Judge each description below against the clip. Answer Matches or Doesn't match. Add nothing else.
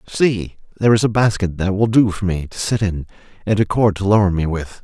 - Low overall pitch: Matches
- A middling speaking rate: Doesn't match